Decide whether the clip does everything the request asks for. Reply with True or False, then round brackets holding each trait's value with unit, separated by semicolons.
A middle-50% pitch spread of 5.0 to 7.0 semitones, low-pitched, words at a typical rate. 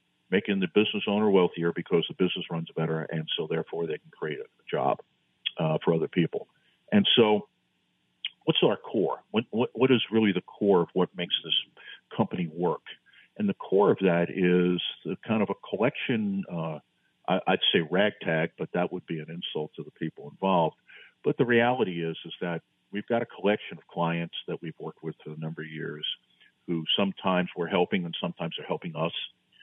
True (5.3 semitones; 90 Hz; 195 wpm)